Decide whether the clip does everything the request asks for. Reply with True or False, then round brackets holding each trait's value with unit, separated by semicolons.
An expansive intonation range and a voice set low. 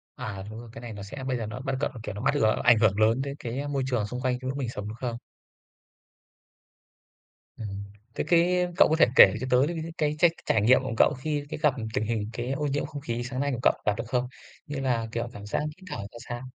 False (4.2 semitones; 125 Hz)